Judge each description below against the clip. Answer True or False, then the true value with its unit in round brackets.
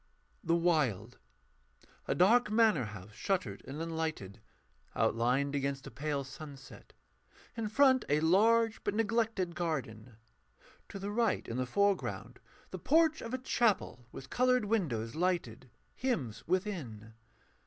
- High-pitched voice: False (165 Hz)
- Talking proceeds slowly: True (130 wpm)